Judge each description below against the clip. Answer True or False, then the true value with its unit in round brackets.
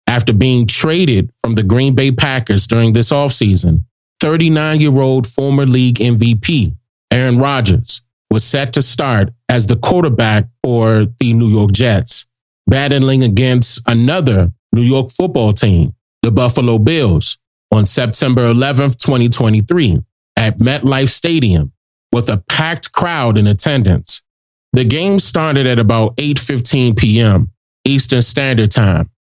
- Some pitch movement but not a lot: True (3.5 semitones)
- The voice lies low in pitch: True (120 Hz)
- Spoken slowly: True (125 wpm)